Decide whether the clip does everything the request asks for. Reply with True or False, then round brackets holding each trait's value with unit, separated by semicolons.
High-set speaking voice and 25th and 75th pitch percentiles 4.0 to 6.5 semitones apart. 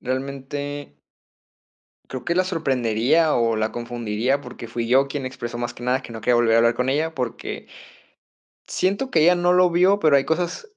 False (135 Hz; 5.3 semitones)